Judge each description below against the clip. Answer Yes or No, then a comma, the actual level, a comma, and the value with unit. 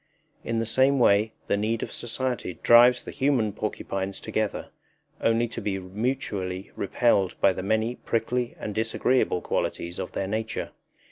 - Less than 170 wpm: Yes, average, 150 wpm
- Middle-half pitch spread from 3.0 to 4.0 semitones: Yes, average, 3.4 semitones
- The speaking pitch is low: Yes, low, 110 Hz